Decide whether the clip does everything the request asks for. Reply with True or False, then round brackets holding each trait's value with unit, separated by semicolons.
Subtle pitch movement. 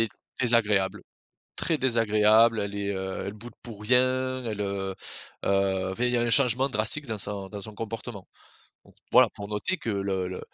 False (3.3 semitones)